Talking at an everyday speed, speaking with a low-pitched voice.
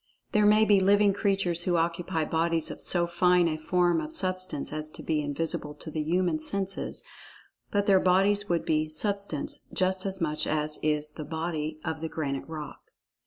No: average, 175 wpm; medium, 170 Hz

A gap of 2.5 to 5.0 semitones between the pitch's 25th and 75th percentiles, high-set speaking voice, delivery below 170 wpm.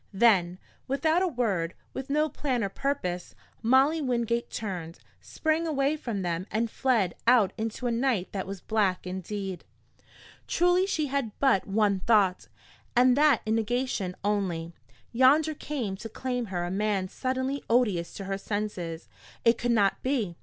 No: wide, 5.4 semitones; high, 225 Hz; average, 155 wpm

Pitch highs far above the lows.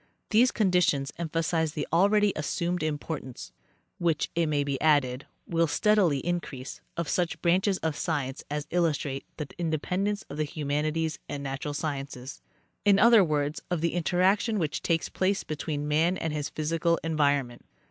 No: average, 3.4 semitones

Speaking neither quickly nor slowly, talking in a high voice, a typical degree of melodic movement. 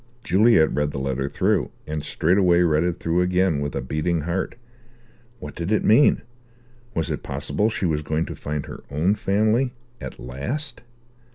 No: average, 170 wpm; very low, 85 Hz; average, 5.0 semitones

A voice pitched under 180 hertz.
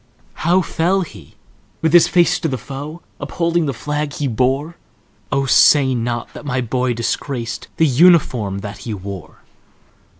Yes: low, 135 Hz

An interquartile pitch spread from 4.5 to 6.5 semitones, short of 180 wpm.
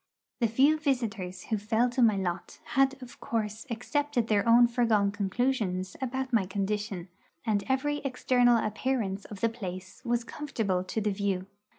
No: average, 3.9 semitones; average, 160 wpm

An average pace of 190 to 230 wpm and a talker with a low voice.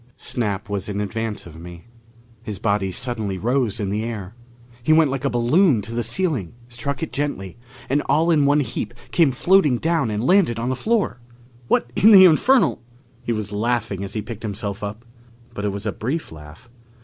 Yes: average, 195 wpm; low, 115 Hz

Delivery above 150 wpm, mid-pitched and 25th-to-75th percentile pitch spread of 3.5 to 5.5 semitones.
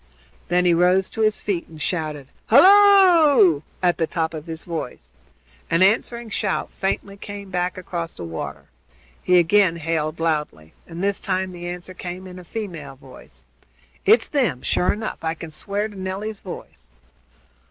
Yes: average, 165 wpm; medium, 180 Hz; average, 3.8 semitones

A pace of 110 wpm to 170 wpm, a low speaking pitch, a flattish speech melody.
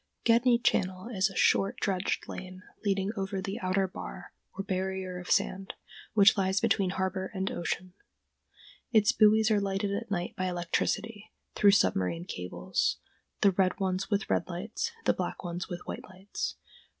No: average, 160 wpm; high, 190 Hz; narrow, 1.7 semitones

